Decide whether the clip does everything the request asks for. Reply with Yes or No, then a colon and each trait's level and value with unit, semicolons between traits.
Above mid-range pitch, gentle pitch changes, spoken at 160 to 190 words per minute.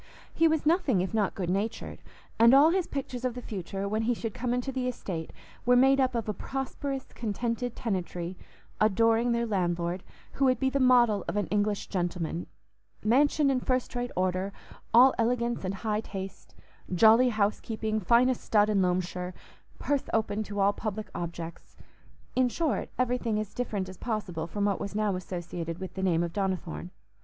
No: high, 215 Hz; average, 4.7 semitones; average, 165 wpm